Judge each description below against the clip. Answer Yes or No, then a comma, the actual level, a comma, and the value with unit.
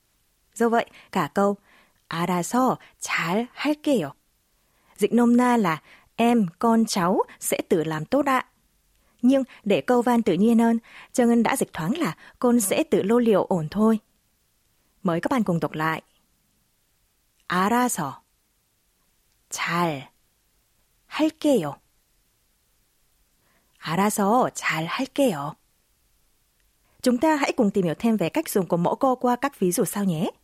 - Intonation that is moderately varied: No, wide, 5.8 semitones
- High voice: Yes, high, 225 Hz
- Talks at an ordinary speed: No, slow, 140 wpm